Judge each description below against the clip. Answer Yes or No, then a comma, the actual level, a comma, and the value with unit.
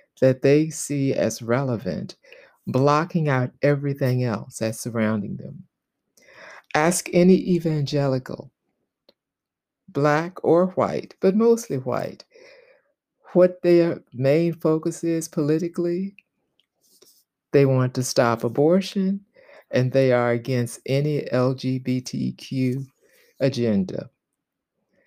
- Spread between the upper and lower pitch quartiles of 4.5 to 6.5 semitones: Yes, average, 5.2 semitones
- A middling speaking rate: No, slow, 95 wpm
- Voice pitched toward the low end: No, medium, 145 Hz